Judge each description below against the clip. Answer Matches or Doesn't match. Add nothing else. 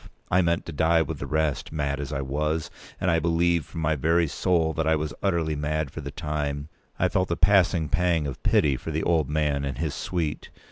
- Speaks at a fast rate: Matches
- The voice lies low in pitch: Matches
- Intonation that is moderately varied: Doesn't match